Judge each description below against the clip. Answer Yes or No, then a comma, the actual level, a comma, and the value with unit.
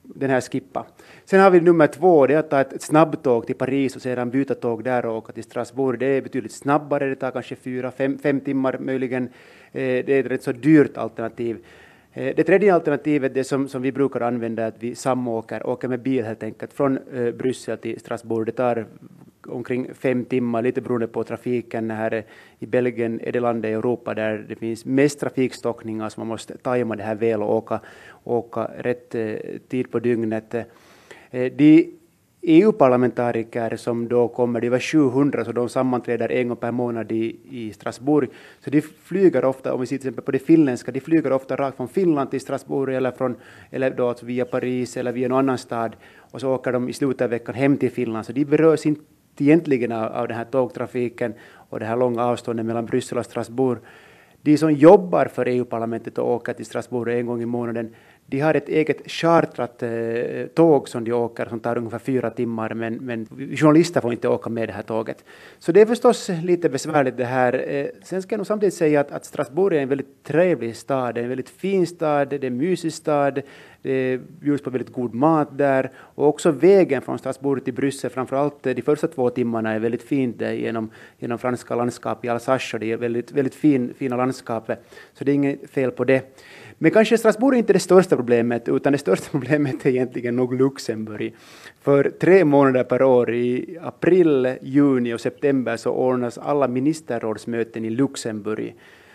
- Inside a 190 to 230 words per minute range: Yes, fast, 195 wpm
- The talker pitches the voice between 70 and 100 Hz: No, low, 125 Hz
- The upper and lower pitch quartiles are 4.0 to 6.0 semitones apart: No, average, 3.0 semitones